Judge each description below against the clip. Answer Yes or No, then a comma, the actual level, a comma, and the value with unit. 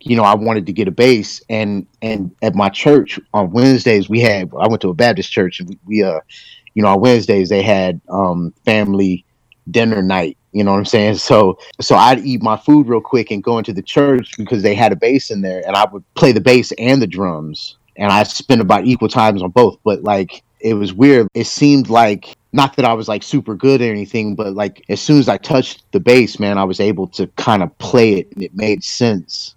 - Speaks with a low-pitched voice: Yes, low, 110 Hz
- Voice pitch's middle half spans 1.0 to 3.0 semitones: No, average, 3.6 semitones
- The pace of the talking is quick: Yes, fast, 240 wpm